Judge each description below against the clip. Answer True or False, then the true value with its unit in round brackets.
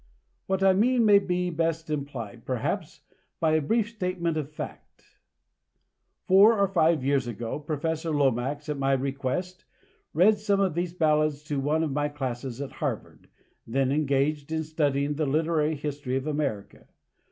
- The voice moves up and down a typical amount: True (3.8 semitones)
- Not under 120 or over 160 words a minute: True (155 wpm)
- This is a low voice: False (150 Hz)